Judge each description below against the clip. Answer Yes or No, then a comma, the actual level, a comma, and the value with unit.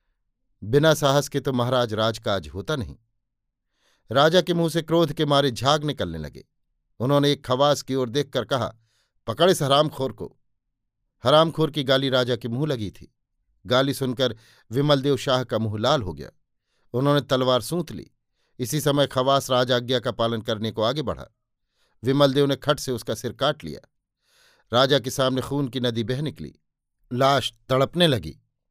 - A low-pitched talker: Yes, low, 130 Hz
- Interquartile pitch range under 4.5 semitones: Yes, average, 3.6 semitones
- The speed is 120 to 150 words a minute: No, average, 165 wpm